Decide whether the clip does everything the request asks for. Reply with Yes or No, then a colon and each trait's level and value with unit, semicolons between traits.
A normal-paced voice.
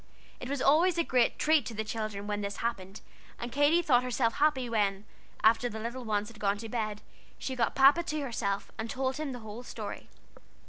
No: fast, 210 wpm